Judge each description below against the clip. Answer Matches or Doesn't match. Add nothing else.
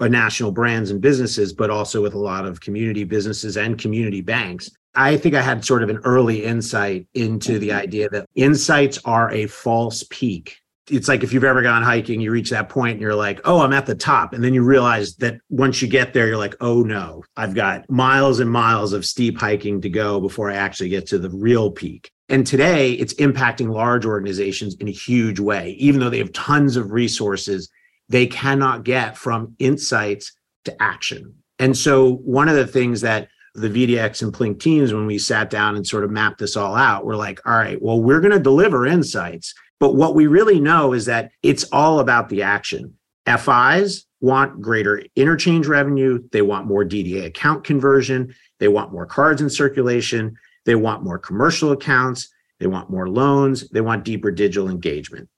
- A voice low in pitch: Matches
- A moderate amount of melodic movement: Matches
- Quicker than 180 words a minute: Matches